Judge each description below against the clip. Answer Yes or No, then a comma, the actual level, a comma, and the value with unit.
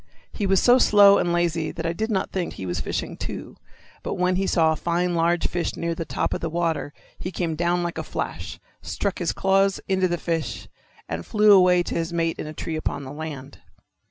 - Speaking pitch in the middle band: Yes, medium, 175 Hz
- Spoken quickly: Yes, fast, 225 wpm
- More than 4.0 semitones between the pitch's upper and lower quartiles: No, narrow, 2.5 semitones